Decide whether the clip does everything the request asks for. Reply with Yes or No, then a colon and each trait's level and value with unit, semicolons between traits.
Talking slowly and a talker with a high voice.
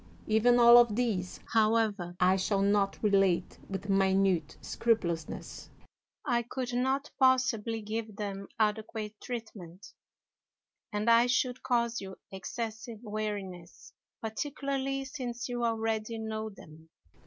Yes: slow, 115 wpm; high, 220 Hz